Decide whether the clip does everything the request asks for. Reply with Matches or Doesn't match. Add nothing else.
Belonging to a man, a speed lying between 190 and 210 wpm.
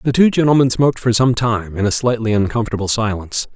Matches